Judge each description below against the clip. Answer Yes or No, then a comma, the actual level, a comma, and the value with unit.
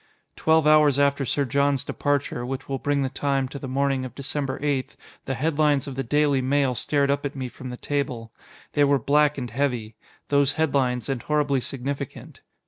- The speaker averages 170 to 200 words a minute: Yes, average, 190 wpm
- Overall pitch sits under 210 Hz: Yes, medium, 140 Hz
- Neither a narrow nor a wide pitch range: No, narrow, 1.6 semitones